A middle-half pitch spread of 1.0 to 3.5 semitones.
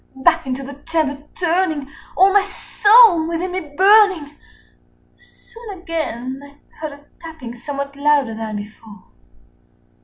No: average, 4.9 semitones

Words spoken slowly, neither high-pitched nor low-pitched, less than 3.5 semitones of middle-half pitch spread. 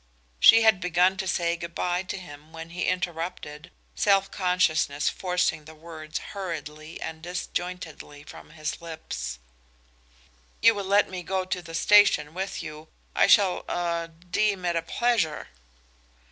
No: average, 145 wpm; medium, 175 Hz; average, 2.8 semitones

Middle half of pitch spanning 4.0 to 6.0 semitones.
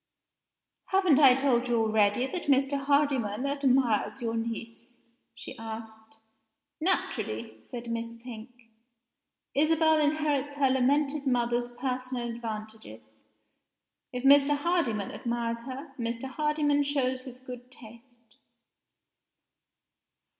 No: average, 3.5 semitones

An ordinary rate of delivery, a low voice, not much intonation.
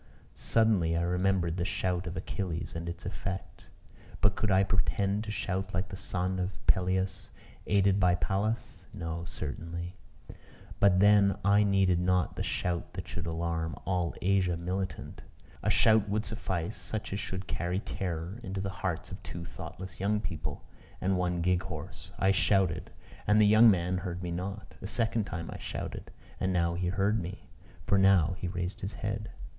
Yes: average, 170 wpm; very low, 95 Hz; narrow, 2.2 semitones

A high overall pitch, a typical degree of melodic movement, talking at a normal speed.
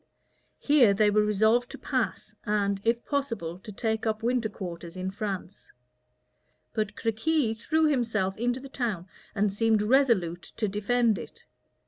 Yes: high, 220 Hz; average, 3.3 semitones; average, 145 wpm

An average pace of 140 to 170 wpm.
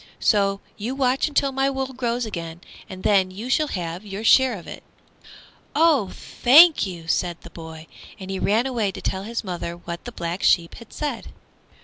No: average, 190 wpm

